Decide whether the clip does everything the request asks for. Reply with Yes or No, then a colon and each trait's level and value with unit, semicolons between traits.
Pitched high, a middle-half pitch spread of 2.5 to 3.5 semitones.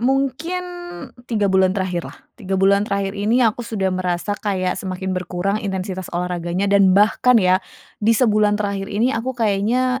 Yes: high, 200 Hz; average, 3.2 semitones